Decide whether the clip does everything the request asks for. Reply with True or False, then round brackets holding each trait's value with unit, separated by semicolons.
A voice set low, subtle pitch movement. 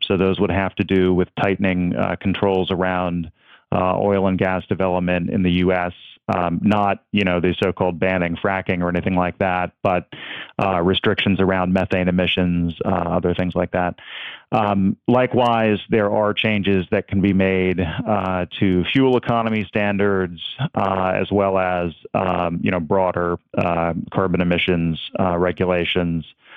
True (95 Hz; 1.7 semitones)